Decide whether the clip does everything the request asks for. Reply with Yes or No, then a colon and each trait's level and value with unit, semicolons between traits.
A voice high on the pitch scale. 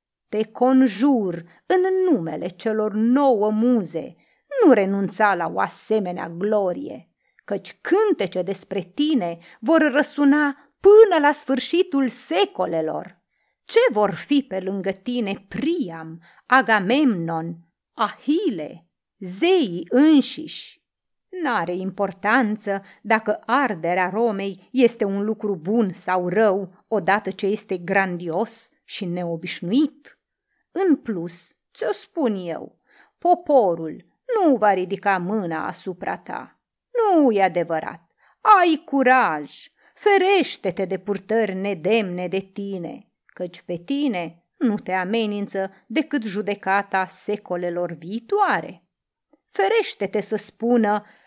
Yes: high, 210 Hz